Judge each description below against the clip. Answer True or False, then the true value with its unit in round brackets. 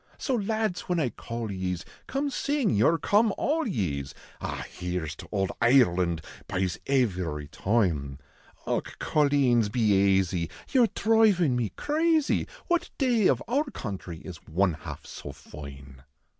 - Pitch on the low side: True (110 Hz)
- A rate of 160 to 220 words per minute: False (150 wpm)